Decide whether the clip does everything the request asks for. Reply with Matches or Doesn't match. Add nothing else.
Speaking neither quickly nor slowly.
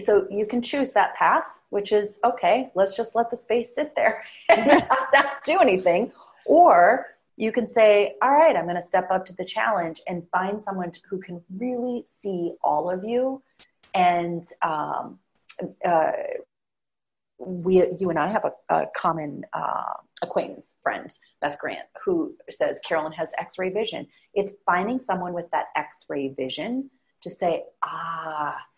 Matches